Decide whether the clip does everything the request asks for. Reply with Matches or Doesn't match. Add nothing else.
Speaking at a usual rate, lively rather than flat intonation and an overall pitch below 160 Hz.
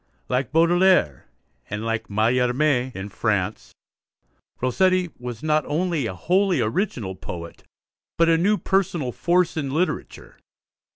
Doesn't match